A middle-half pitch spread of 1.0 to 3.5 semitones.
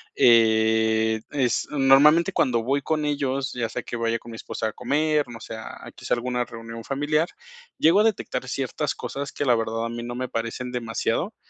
No: average, 3.9 semitones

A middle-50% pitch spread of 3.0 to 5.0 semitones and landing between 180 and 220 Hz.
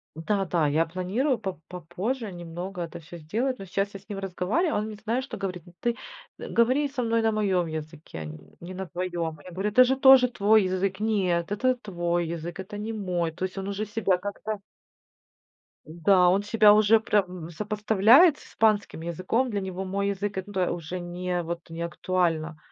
Yes: average, 3.7 semitones; high, 190 Hz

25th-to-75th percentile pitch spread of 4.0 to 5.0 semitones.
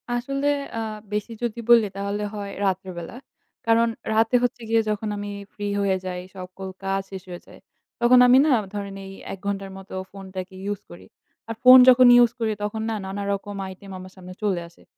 No: average, 2.9 semitones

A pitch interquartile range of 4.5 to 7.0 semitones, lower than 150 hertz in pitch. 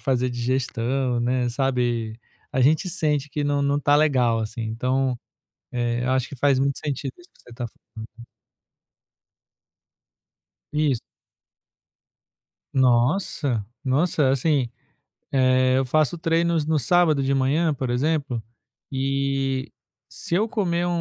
No: average, 3.2 semitones; low, 135 Hz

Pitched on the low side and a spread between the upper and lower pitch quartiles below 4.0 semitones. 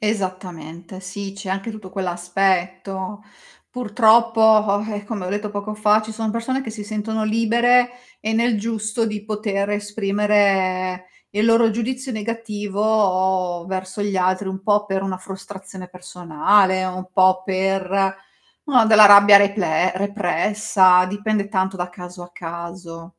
No: high, 200 Hz; narrow, 2.5 semitones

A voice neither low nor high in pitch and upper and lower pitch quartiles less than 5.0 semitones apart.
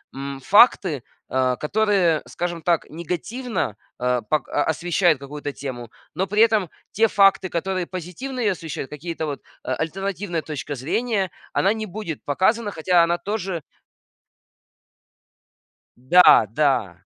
No: medium, 170 Hz; average, 5.3 semitones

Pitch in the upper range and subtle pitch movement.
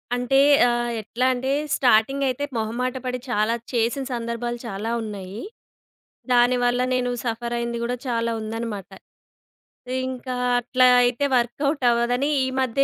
Yes: high, 240 Hz; narrow, 1.5 semitones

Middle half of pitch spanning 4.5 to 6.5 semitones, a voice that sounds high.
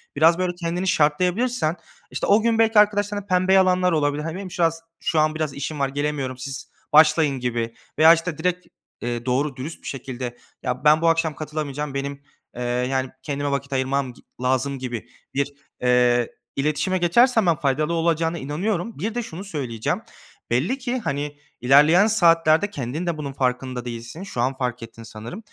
No: average, 5.0 semitones; medium, 150 Hz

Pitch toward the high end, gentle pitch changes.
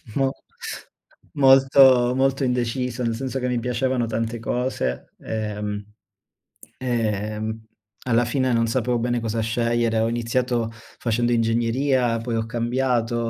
No: low, 120 Hz; narrow, 1.9 semitones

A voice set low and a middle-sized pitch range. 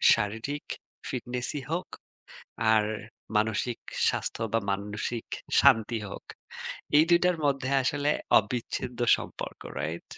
Yes: low, 120 Hz; average, 4.5 semitones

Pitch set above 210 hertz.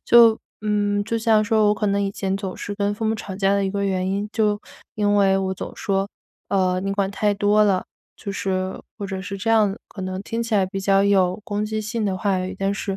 No: high, 200 Hz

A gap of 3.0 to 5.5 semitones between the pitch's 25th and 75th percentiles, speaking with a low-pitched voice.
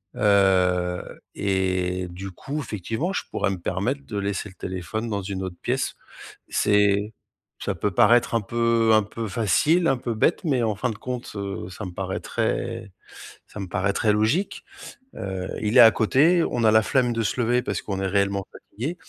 Yes: average, 3.6 semitones; low, 105 Hz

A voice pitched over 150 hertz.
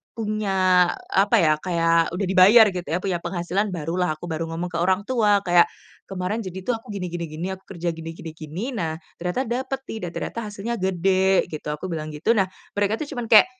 Yes: medium, 185 Hz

